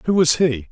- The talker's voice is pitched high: No, medium, 150 Hz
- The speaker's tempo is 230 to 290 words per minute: Yes, fast, 250 wpm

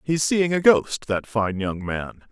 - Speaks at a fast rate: No, average, 180 wpm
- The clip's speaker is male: Yes, male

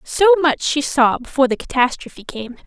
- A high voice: Yes, very high, 275 Hz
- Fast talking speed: No, average, 180 wpm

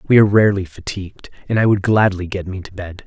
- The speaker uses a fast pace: Yes, fast, 235 wpm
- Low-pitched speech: Yes, very low, 95 Hz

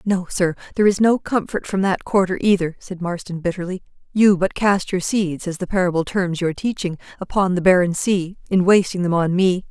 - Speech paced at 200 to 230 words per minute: Yes, fast, 205 wpm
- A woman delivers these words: Yes, female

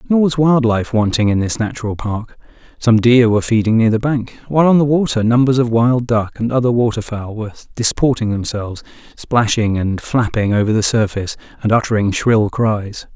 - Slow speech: No, average, 185 wpm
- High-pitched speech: No, low, 115 Hz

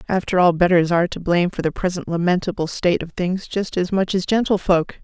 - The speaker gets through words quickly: Yes, fast, 215 wpm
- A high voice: No, medium, 180 Hz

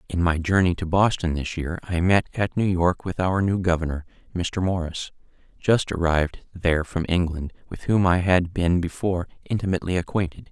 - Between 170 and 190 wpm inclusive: Yes, average, 175 wpm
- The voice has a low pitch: Yes, very low, 90 Hz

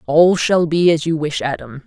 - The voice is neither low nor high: Yes, medium, 160 Hz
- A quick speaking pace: Yes, fast, 225 wpm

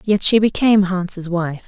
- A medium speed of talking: Yes, average, 180 wpm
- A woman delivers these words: Yes, female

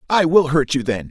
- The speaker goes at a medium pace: No, fast, 270 wpm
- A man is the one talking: Yes, male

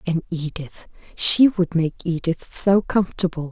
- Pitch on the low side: No, medium, 175 Hz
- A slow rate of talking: Yes, slow, 120 wpm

